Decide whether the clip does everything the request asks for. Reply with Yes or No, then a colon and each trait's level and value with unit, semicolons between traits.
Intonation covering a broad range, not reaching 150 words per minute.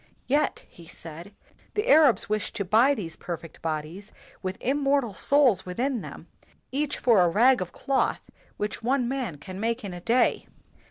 No: wide, 6.7 semitones; average, 165 wpm